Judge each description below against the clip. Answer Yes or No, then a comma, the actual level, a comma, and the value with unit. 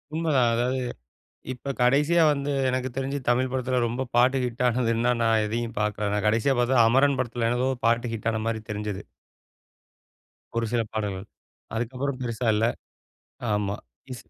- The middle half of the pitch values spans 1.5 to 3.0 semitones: Yes, average, 2.7 semitones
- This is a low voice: Yes, low, 120 Hz